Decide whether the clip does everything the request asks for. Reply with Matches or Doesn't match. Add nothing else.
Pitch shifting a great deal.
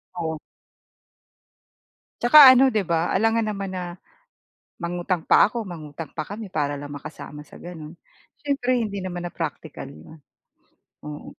Matches